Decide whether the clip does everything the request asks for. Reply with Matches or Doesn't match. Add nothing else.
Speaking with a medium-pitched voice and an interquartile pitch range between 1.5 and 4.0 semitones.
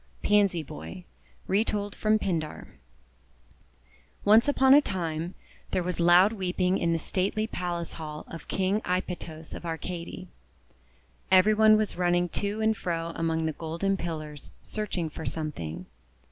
Matches